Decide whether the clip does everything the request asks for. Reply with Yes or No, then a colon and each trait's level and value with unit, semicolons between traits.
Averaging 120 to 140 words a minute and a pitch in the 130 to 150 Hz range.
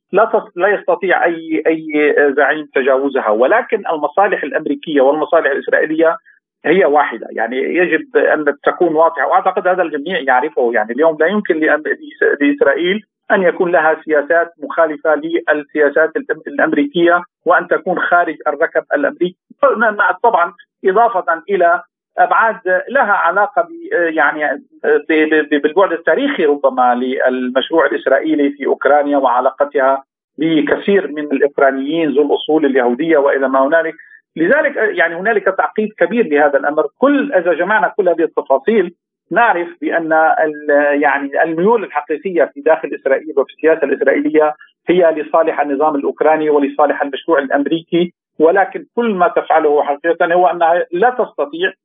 No: average, 125 wpm; medium, 160 Hz